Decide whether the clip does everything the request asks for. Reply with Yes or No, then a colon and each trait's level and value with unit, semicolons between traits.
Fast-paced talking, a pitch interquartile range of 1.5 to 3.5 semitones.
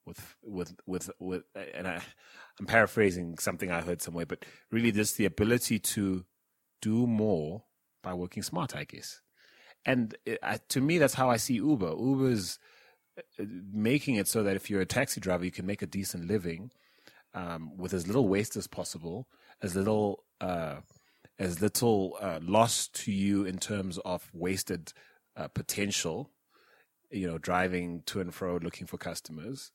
No: average, 165 wpm; average, 3.2 semitones